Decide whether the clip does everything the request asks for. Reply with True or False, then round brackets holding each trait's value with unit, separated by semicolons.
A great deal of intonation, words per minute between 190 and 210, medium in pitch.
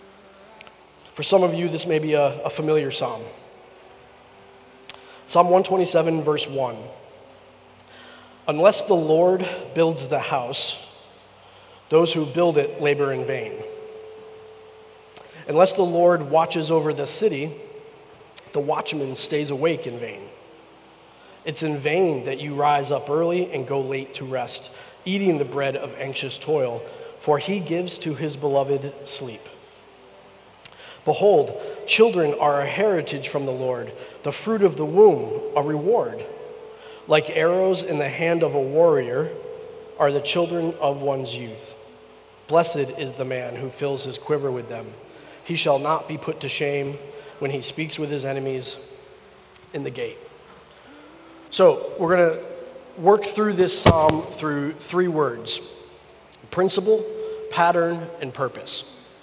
False (6.4 semitones; 140 wpm; 160 Hz)